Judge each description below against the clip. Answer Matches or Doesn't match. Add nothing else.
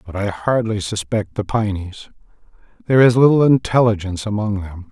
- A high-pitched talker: Doesn't match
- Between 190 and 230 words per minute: Doesn't match